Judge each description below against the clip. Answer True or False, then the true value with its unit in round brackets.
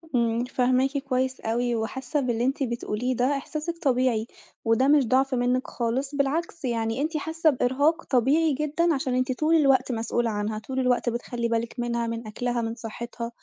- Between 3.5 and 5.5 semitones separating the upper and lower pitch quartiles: False (3.0 semitones)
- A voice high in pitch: True (255 Hz)